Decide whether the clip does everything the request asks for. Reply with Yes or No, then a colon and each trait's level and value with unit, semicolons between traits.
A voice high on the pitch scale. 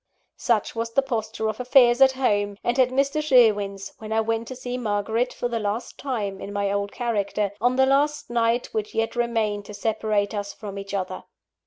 Yes: high, 225 Hz